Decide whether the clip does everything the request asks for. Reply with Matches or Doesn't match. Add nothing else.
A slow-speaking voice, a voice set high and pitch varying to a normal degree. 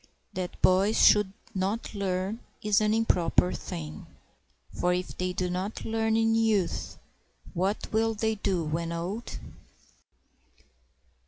Matches